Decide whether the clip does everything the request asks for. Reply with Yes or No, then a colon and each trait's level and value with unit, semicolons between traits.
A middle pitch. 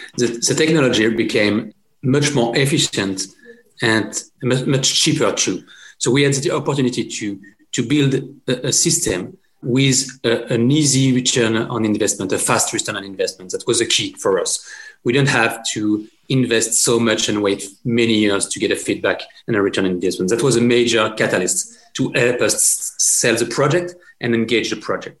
No: low, 125 Hz